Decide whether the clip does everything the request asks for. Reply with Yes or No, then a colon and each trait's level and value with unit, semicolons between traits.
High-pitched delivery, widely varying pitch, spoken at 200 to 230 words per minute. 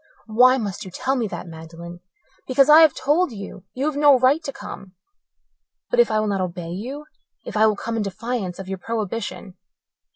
Yes: high, 220 Hz; wide, 5.9 semitones; fast, 205 wpm